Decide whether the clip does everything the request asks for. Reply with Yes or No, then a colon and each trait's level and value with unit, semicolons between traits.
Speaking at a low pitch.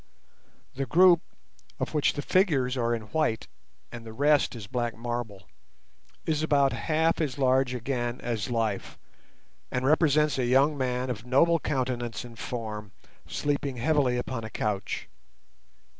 Yes: low, 125 Hz